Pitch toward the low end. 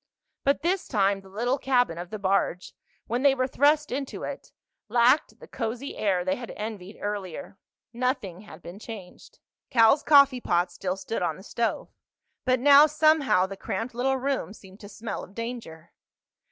No: high, 230 Hz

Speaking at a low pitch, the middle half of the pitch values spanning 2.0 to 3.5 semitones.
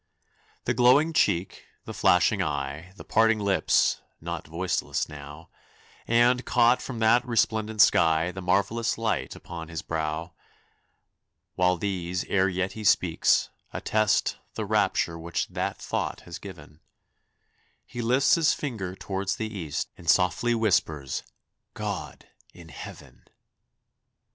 No: very low, 95 Hz; average, 5.3 semitones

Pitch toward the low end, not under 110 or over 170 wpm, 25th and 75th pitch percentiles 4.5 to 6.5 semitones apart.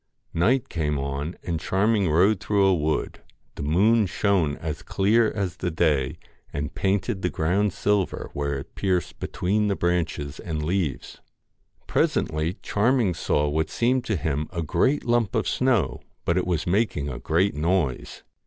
Yes: very low, 90 Hz; average, 160 wpm; average, 4.9 semitones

